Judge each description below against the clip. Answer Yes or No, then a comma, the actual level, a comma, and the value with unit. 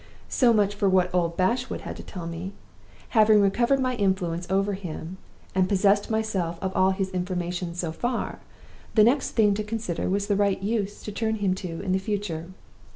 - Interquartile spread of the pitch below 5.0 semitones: Yes, average, 2.8 semitones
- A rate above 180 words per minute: Yes, average, 190 wpm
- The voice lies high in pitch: Yes, high, 195 Hz